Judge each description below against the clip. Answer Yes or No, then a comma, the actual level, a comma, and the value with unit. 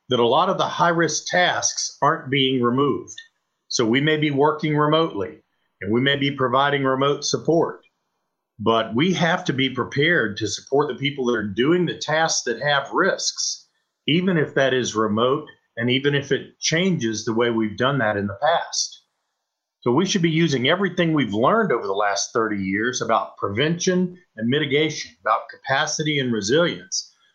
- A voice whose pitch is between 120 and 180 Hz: Yes, medium, 140 Hz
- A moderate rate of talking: Yes, average, 180 wpm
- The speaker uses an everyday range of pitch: Yes, average, 4.9 semitones